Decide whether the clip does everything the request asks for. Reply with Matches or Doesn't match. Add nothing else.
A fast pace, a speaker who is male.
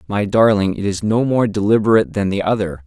Matches